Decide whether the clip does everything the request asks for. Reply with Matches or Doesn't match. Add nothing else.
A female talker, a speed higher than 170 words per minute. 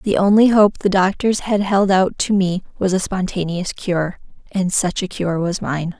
Matches